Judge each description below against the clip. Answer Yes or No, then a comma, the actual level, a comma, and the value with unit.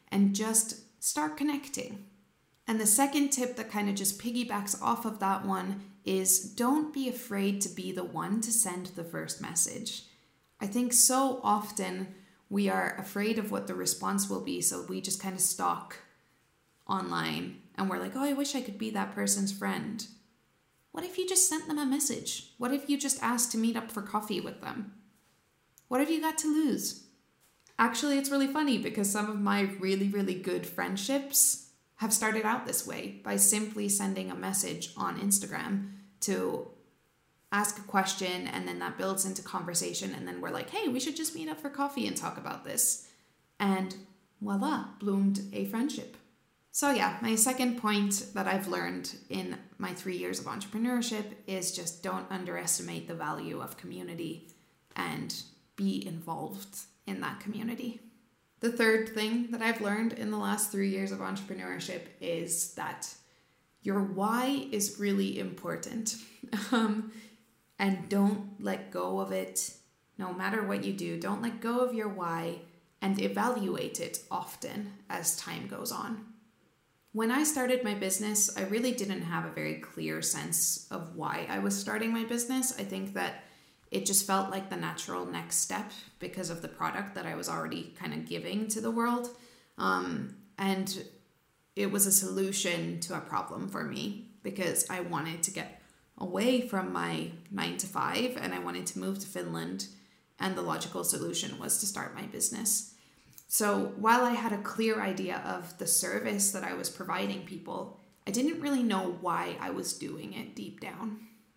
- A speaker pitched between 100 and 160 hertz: No, high, 205 Hz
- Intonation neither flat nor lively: Yes, average, 3.6 semitones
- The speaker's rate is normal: Yes, average, 175 wpm